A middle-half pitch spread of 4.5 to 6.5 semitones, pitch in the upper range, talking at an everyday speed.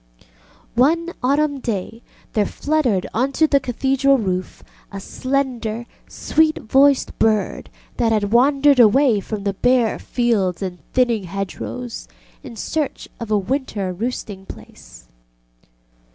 No: average, 4.9 semitones; high, 240 Hz; slow, 125 wpm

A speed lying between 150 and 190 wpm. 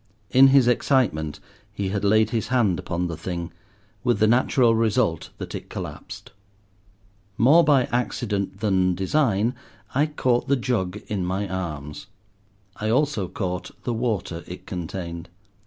No: average, 140 wpm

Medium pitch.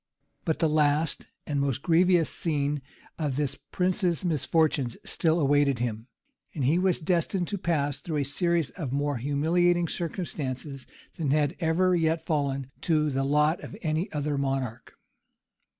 Yes: medium, 150 Hz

